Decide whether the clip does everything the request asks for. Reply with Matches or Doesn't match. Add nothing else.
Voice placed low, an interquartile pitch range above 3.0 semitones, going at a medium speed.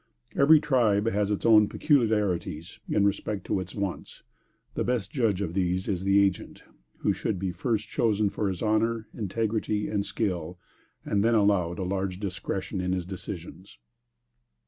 Doesn't match